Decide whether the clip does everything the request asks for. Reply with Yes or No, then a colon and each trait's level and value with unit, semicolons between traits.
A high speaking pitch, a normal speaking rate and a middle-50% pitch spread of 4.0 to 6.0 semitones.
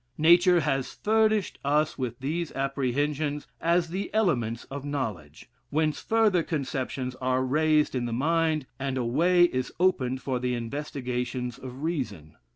No: medium, 140 Hz; average, 145 wpm; average, 4.5 semitones